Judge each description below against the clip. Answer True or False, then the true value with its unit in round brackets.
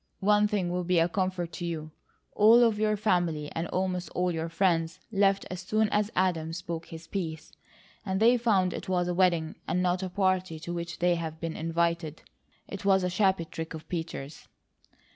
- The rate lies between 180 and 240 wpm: True (195 wpm)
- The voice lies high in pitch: False (180 Hz)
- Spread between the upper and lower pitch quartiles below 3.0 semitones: True (2.5 semitones)